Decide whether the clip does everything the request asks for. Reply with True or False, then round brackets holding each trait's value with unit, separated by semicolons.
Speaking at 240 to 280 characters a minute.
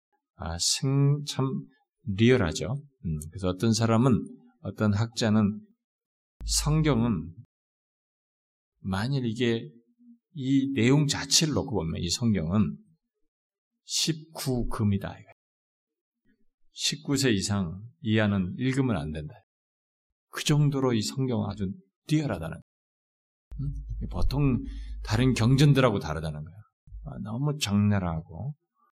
False (200 characters per minute)